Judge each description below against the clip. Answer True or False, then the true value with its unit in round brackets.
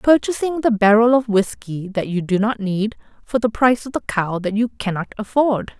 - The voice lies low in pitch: False (220 Hz)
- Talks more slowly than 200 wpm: False (205 wpm)